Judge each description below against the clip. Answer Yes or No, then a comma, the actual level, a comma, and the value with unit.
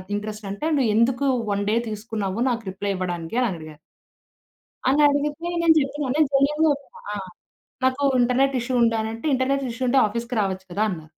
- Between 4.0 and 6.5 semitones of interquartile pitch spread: Yes, average, 5.2 semitones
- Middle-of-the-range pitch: No, high, 235 Hz